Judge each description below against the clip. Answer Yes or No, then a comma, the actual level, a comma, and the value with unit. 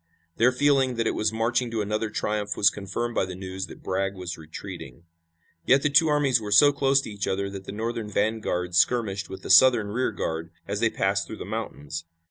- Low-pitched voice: Yes, low, 105 Hz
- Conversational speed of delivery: No, fast, 210 wpm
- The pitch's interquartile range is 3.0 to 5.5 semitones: Yes, average, 3.8 semitones